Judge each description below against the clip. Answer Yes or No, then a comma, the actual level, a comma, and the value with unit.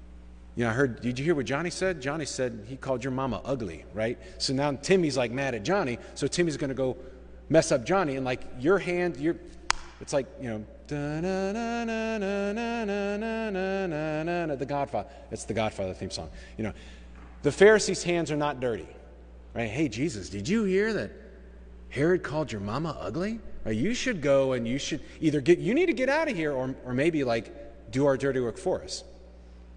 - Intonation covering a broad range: Yes, wide, 8.2 semitones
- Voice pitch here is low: No, medium, 145 Hz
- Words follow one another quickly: No, average, 190 wpm